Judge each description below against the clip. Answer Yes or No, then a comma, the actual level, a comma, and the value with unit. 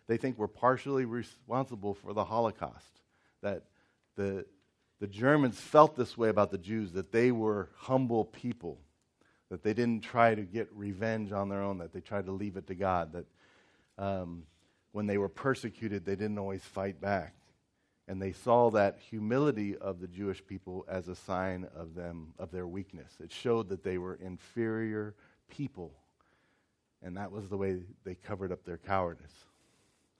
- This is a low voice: Yes, low, 100 Hz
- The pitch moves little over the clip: No, average, 3.4 semitones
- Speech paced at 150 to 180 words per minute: Yes, average, 170 wpm